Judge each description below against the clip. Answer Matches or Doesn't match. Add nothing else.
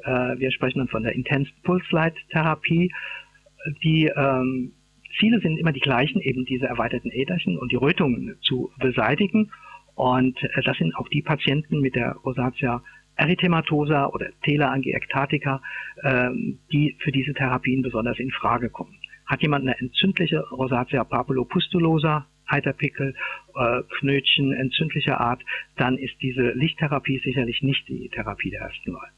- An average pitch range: Matches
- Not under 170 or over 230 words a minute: Doesn't match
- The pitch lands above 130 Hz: Matches